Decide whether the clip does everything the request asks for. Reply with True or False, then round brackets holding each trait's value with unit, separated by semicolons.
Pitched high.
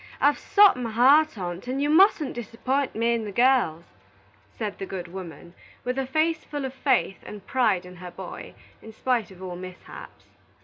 True (230 Hz)